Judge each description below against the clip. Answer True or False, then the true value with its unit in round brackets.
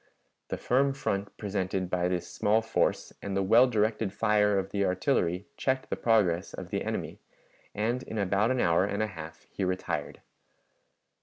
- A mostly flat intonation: False (3.3 semitones)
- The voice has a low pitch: True (100 Hz)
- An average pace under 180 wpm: True (170 wpm)